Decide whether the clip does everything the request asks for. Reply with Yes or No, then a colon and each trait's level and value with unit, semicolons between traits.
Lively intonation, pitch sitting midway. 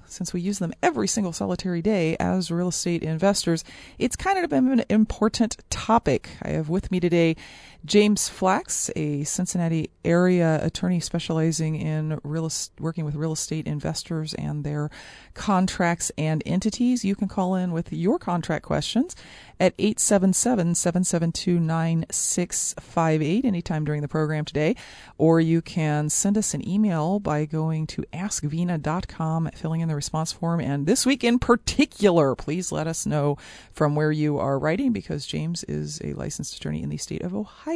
No: average, 3.5 semitones; medium, 165 Hz